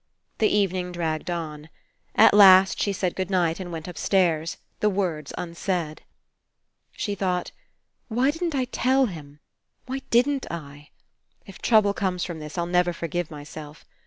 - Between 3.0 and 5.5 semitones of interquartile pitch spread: Yes, average, 4.0 semitones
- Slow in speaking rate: No, average, 150 wpm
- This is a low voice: No, medium, 180 Hz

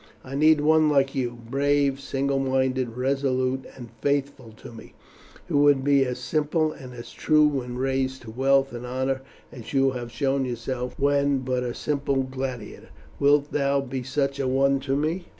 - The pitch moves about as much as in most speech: No, narrow, 1.7 semitones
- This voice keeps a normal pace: Yes, average, 175 wpm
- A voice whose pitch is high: No, low, 135 Hz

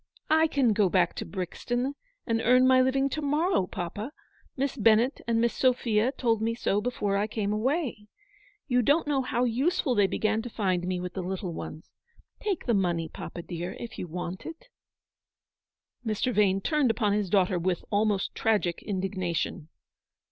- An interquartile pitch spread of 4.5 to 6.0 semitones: Yes, average, 5.3 semitones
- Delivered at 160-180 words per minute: Yes, average, 170 wpm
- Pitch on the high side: Yes, high, 220 Hz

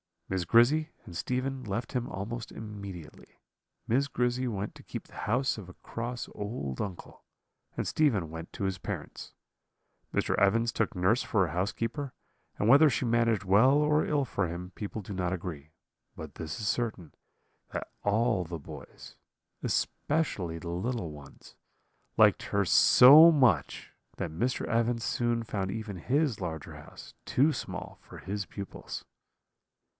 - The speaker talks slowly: No, average, 150 wpm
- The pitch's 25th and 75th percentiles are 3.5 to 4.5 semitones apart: No, wide, 5.4 semitones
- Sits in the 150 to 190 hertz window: No, low, 110 Hz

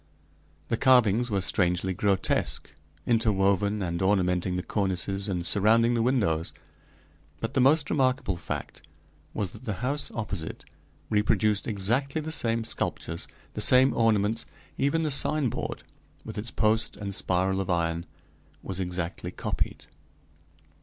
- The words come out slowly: Yes, slow, 130 wpm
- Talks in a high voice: No, low, 105 Hz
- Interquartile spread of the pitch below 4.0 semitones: No, average, 4.3 semitones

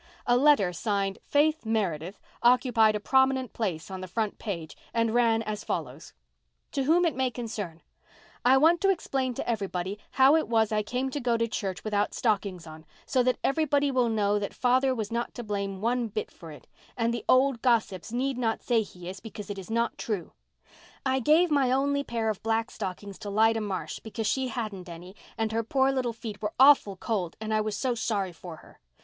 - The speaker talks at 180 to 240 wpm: Yes, fast, 205 wpm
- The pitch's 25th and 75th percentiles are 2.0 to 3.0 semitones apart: No, average, 4.1 semitones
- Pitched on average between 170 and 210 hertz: No, high, 225 Hz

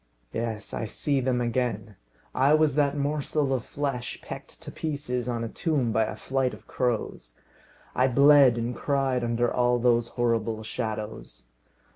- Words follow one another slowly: No, average, 155 wpm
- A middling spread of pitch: Yes, average, 3.1 semitones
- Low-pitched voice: Yes, low, 125 Hz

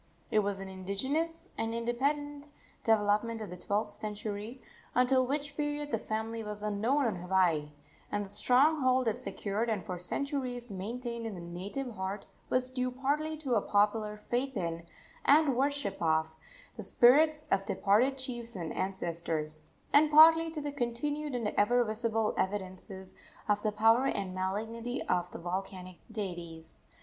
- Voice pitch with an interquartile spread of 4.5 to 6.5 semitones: Yes, average, 5.1 semitones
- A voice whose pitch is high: Yes, high, 225 Hz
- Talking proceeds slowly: No, average, 155 wpm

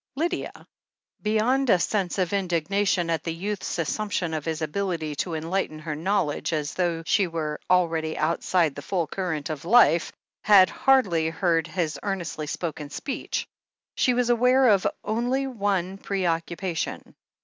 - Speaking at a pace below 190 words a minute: Yes, average, 140 wpm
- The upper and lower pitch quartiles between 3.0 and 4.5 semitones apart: Yes, average, 4.2 semitones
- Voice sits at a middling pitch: Yes, medium, 180 Hz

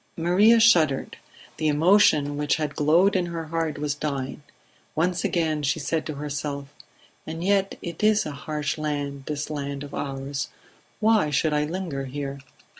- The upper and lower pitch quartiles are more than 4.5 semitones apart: No, average, 3.0 semitones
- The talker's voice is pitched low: No, medium, 150 Hz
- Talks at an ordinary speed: Yes, average, 160 wpm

